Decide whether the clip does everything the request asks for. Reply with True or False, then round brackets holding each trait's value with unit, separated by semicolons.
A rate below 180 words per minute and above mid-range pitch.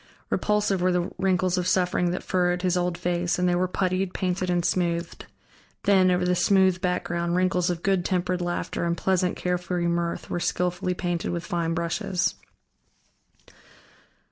False (160 wpm; 180 Hz)